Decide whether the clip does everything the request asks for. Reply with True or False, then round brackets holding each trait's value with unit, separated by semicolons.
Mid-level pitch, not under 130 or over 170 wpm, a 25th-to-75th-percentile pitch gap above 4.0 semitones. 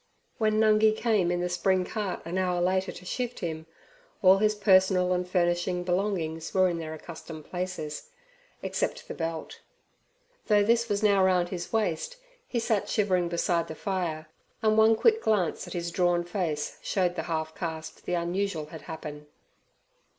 False (180 Hz; 165 wpm; 3.1 semitones)